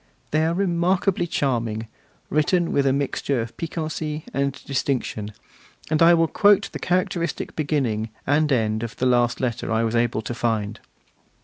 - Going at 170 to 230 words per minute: No, average, 155 wpm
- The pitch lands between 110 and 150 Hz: Yes, medium, 140 Hz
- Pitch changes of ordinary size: No, wide, 6.1 semitones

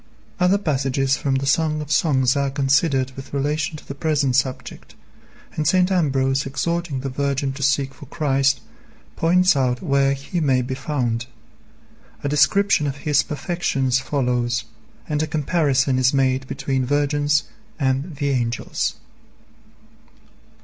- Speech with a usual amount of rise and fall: No, narrow, 2.3 semitones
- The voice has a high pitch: No, medium, 140 Hz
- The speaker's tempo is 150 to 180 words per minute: No, average, 140 wpm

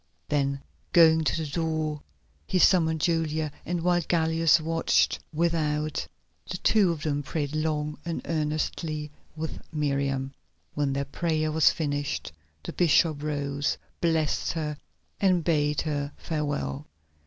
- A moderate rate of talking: No, slow, 130 wpm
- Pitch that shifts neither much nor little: No, narrow, 2.0 semitones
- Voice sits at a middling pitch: Yes, medium, 155 Hz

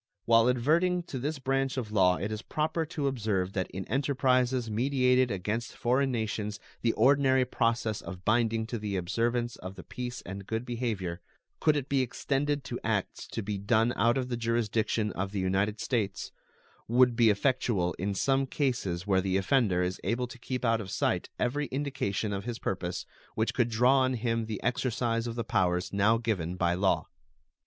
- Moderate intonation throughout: Yes, average, 4.1 semitones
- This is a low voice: Yes, low, 115 Hz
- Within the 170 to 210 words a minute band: Yes, average, 185 wpm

